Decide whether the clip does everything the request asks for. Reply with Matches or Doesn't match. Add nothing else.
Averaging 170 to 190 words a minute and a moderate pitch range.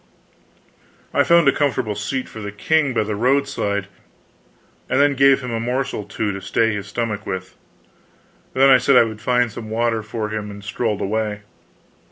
Matches